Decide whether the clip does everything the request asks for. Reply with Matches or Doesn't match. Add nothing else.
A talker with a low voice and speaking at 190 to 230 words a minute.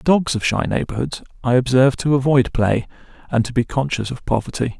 Matches